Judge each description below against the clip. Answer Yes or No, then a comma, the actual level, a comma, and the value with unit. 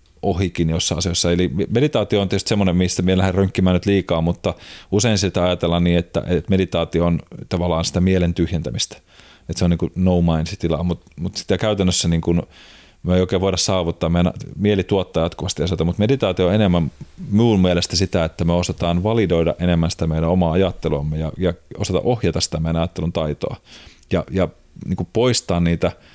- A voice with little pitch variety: Yes, narrow, 2.2 semitones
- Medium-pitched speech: No, very low, 90 Hz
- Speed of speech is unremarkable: No, fast, 180 wpm